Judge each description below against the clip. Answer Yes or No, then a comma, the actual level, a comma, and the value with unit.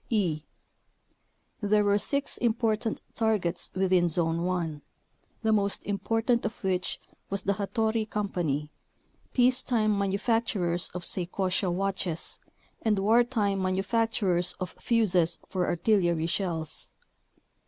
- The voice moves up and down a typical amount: Yes, average, 3.6 semitones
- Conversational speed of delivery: No, slow, 110 wpm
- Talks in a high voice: Yes, high, 200 Hz